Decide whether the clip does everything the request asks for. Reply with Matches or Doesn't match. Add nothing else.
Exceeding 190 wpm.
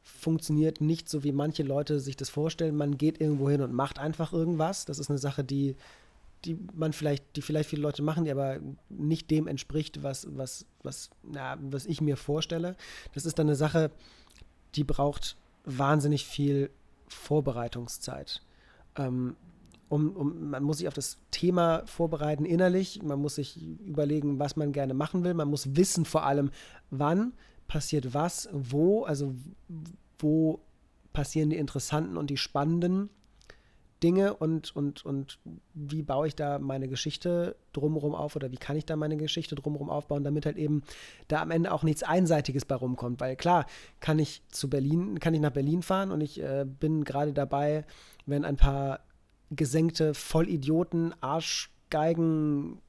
Doesn't match